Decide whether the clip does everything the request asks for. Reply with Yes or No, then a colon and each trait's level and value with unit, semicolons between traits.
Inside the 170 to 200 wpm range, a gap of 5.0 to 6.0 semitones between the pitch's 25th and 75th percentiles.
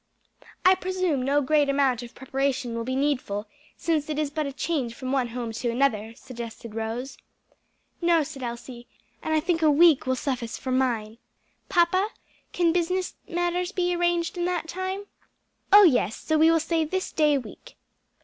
Yes: average, 175 wpm; wide, 5.6 semitones